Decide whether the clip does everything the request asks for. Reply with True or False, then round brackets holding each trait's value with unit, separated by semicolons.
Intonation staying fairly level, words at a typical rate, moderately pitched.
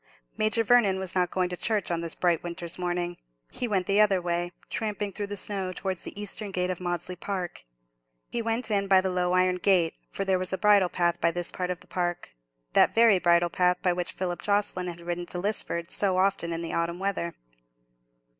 False (2.3 semitones; 210 wpm; 180 Hz)